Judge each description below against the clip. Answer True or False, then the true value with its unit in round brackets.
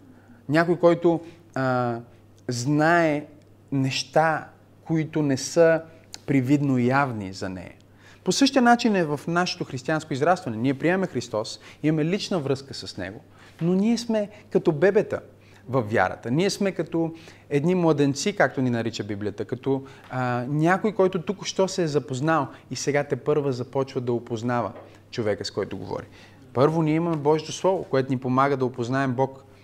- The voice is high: False (140 Hz)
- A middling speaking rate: True (150 wpm)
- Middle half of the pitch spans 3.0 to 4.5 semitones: False (5.6 semitones)